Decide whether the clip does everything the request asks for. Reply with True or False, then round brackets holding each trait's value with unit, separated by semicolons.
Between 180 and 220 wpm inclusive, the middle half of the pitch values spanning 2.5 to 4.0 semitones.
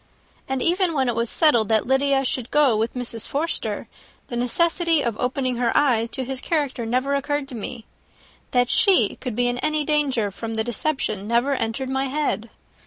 True (185 wpm; 3.6 semitones)